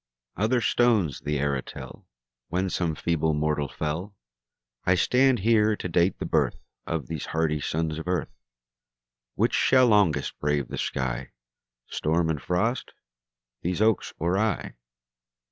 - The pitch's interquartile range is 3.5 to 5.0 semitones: No, wide, 5.5 semitones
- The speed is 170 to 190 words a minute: No, average, 140 wpm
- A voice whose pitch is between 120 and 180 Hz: No, very low, 85 Hz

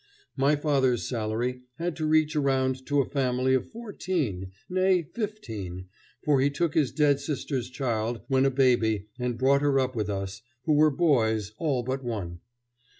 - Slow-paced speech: No, average, 165 wpm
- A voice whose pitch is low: Yes, low, 130 Hz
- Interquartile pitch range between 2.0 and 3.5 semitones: No, average, 4.4 semitones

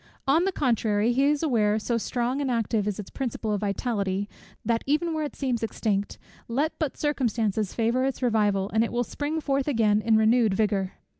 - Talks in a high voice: Yes, high, 230 Hz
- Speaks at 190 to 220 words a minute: Yes, average, 195 wpm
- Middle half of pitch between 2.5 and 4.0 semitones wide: No, average, 4.4 semitones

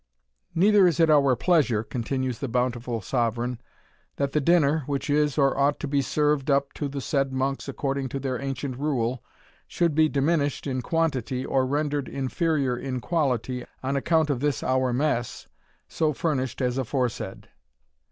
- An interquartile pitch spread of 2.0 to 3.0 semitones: Yes, narrow, 2.6 semitones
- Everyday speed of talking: Yes, average, 160 wpm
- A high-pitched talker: No, low, 135 Hz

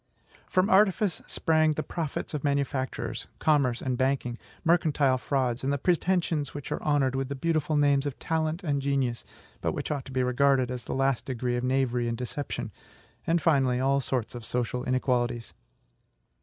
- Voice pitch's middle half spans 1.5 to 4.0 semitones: Yes, average, 3.2 semitones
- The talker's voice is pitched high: No, low, 135 Hz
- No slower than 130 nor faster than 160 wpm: No, average, 170 wpm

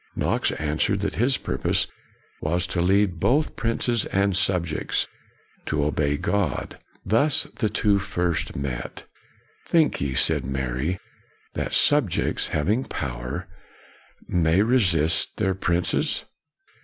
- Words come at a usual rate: No, slow, 120 wpm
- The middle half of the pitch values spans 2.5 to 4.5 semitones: No, wide, 5.4 semitones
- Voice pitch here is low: Yes, very low, 90 Hz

